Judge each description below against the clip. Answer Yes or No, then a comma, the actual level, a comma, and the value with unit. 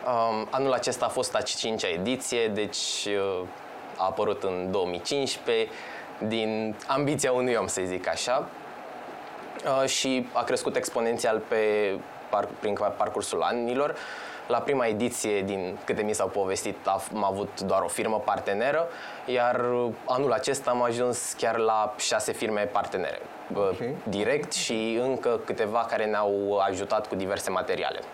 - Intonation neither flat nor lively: Yes, average, 3.4 semitones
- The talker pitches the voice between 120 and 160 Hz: No, low, 110 Hz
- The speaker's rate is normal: Yes, average, 130 wpm